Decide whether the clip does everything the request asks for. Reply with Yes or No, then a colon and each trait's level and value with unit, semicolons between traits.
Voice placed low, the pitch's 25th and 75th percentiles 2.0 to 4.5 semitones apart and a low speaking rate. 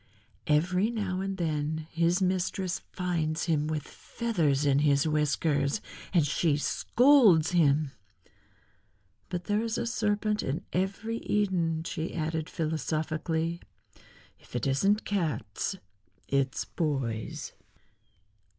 No: medium, 165 Hz; average, 4.0 semitones; slow, 110 wpm